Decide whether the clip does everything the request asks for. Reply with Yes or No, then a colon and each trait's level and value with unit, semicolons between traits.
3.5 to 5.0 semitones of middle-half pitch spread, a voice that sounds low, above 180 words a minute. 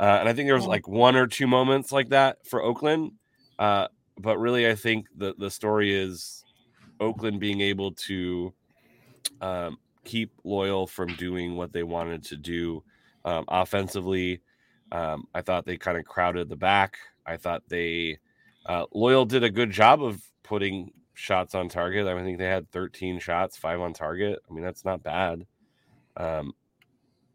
No: average, 3.9 semitones; very low, 95 Hz; average, 175 wpm